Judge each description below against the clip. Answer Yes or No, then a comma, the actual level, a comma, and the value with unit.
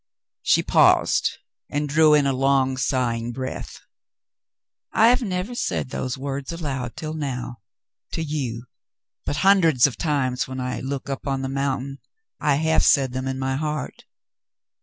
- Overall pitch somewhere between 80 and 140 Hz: Yes, low, 135 Hz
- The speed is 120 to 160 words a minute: Yes, average, 155 wpm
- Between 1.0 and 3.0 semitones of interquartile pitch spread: Yes, average, 2.7 semitones